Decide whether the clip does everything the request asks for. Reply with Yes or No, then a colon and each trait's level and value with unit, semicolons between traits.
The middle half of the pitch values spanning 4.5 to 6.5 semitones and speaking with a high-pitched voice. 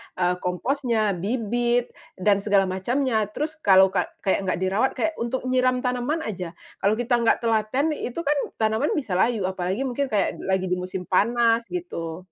Yes: average, 4.9 semitones; high, 225 Hz